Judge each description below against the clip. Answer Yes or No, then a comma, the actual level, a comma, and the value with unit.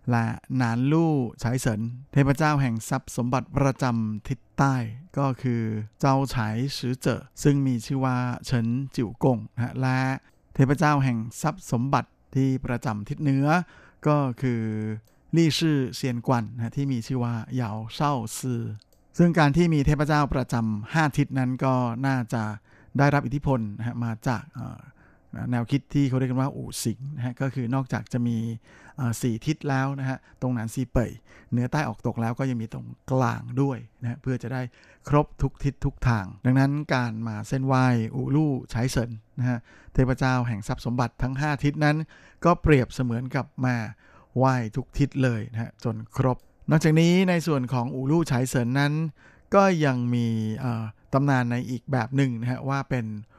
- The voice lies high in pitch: No, low, 130 Hz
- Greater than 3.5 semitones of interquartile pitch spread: No, average, 2.9 semitones